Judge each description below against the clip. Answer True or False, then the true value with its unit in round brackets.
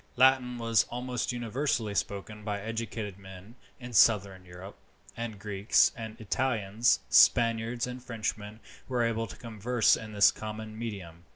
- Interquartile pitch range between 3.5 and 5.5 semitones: False (2.6 semitones)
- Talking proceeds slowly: True (130 wpm)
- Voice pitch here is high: False (110 Hz)